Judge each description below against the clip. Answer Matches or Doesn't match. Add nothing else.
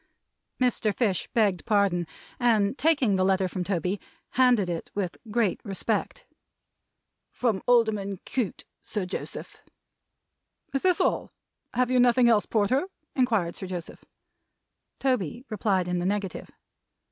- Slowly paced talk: Matches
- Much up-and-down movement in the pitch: Doesn't match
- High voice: Matches